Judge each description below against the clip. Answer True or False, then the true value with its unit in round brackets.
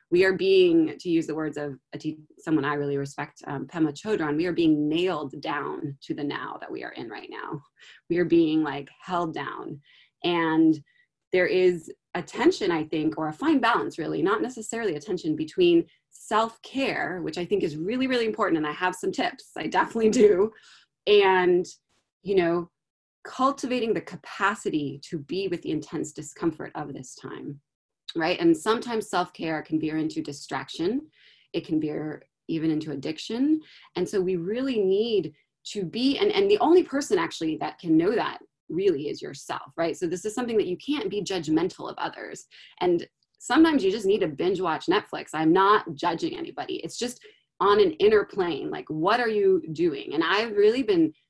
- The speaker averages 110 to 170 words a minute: False (185 wpm)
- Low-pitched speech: False (210 Hz)